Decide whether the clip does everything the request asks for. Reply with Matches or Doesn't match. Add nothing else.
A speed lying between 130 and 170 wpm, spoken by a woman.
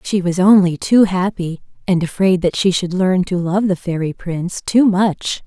Doesn't match